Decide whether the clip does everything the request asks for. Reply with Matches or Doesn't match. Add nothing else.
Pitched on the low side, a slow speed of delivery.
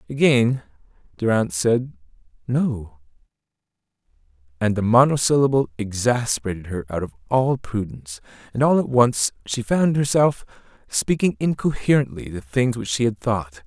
Matches